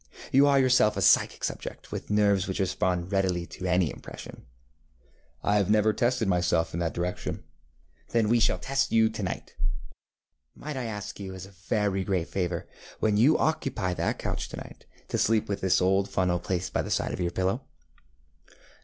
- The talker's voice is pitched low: Yes, very low, 95 Hz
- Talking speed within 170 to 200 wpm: Yes, average, 180 wpm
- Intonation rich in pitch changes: No, average, 3.5 semitones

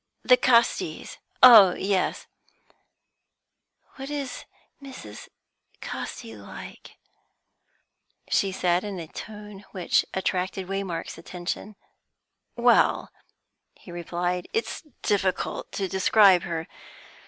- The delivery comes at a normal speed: No, slow, 90 wpm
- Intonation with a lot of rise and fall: No, average, 3.3 semitones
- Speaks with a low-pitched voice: No, high, 190 Hz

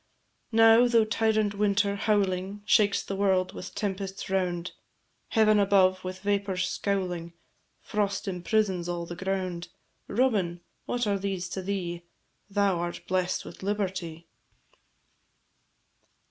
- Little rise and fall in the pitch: Yes, narrow, 2.1 semitones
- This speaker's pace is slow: Yes, slow, 120 wpm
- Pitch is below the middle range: No, high, 195 Hz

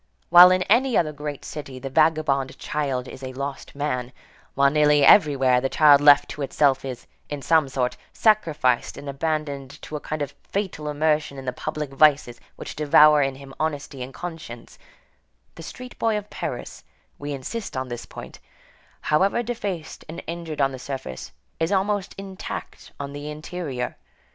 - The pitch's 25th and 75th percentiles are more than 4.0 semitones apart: No, average, 3.1 semitones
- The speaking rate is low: No, average, 170 wpm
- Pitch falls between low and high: Yes, medium, 150 Hz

